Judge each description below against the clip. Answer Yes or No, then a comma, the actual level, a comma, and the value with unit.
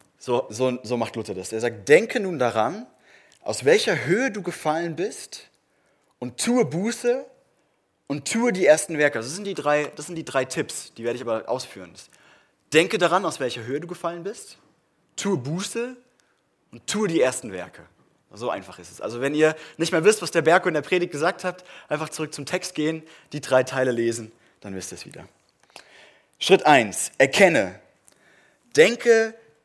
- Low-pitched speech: No, medium, 160 Hz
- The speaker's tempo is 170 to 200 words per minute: Yes, average, 185 wpm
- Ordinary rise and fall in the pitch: No, wide, 6.6 semitones